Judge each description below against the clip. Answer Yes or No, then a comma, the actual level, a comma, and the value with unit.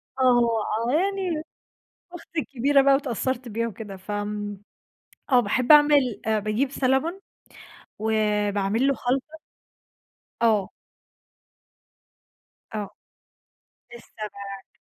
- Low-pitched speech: No, high, 240 Hz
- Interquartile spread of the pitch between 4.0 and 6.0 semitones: Yes, average, 4.7 semitones